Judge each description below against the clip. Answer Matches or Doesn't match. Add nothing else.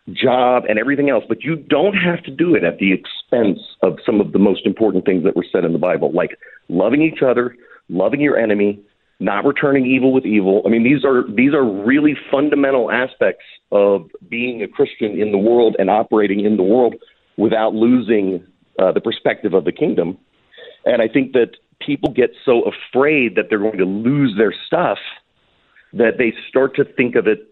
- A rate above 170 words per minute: Matches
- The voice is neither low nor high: Doesn't match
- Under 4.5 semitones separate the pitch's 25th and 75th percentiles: Doesn't match